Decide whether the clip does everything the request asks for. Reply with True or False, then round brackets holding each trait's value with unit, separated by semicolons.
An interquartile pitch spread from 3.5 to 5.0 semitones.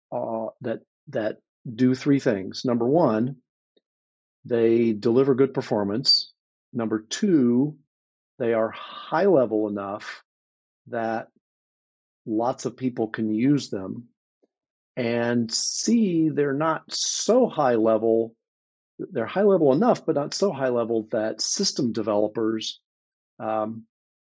True (4.0 semitones)